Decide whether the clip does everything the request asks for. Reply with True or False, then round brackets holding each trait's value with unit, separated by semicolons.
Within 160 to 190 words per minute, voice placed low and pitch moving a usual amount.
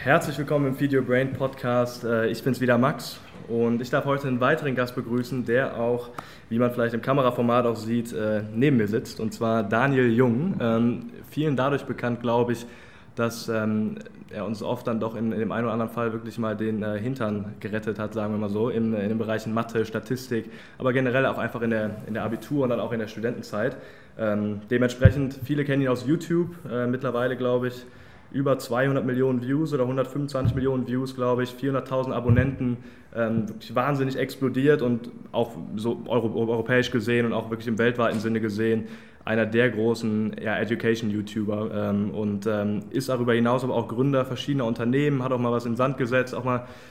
False (185 wpm; 120 Hz; 2.3 semitones)